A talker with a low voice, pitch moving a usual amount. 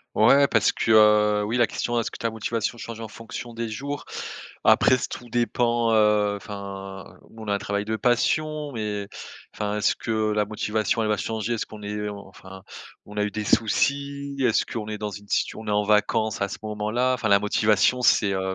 No: low, 110 Hz; narrow, 2.1 semitones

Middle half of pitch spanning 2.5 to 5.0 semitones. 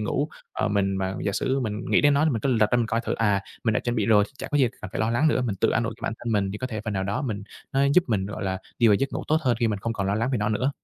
Yes: average, 3.6 semitones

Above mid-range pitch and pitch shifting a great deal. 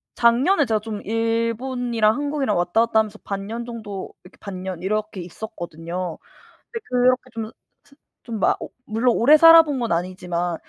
No: high, 220 Hz; average, 4.5 semitones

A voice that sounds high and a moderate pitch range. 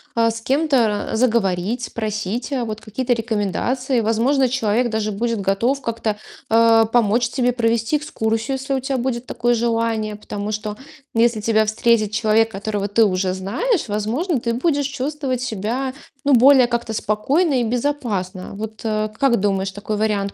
Yes: high, 230 Hz; average, 3.0 semitones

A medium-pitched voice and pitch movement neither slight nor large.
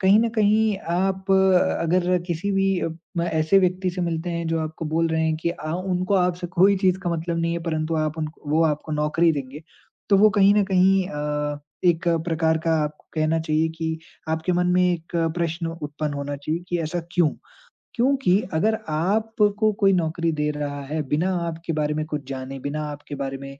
Yes: medium, 165 Hz; average, 3.2 semitones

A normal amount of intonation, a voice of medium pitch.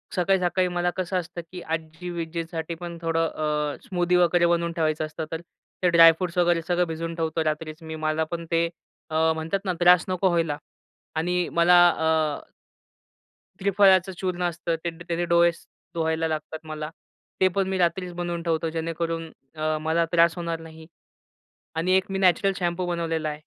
No: narrow, 1.7 semitones; medium, 170 Hz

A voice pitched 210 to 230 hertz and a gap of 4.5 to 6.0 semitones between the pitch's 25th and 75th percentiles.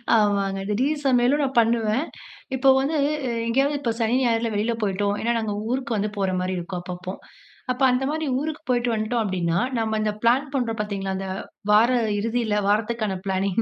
No: high, 225 Hz; average, 3.7 semitones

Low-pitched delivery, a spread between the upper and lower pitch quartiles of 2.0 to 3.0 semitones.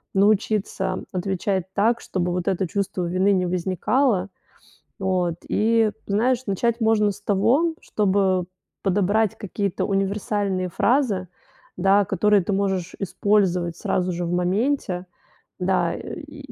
No: high, 195 Hz; narrow, 2.6 semitones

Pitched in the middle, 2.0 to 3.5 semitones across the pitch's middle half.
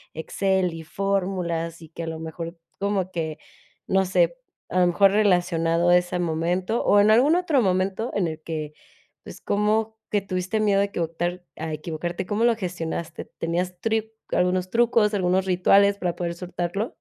Yes: medium, 180 Hz; average, 3.1 semitones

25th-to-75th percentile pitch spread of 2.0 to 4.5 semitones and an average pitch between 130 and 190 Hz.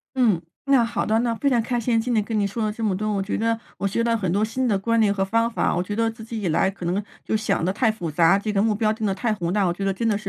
No: average, 2.8 semitones; high, 215 Hz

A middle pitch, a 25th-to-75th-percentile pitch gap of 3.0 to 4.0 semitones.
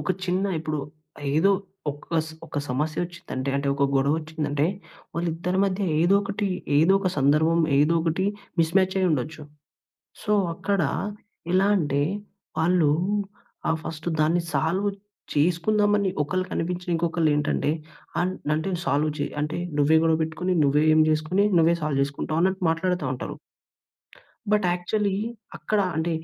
Yes: medium, 165 Hz; average, 3.3 semitones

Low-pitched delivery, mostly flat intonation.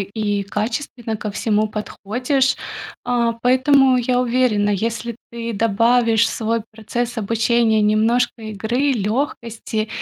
No: high, 230 Hz; narrow, 2.3 semitones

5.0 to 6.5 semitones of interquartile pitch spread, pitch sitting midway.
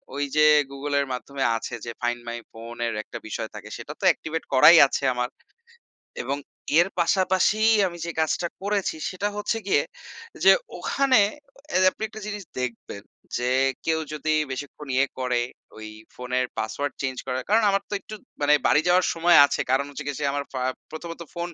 Yes: wide, 5.6 semitones; medium, 145 Hz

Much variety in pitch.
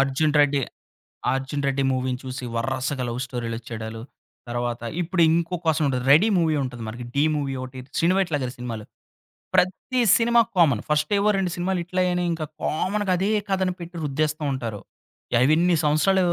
Yes: wide, 5.8 semitones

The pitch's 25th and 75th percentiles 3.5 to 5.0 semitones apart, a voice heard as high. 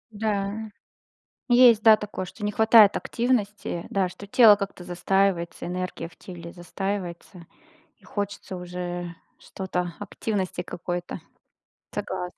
No: average, 2.7 semitones; high, 195 Hz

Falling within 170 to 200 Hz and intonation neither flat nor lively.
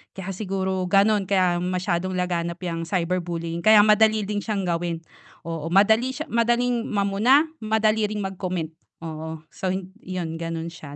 Yes: medium, 185 Hz; average, 3.9 semitones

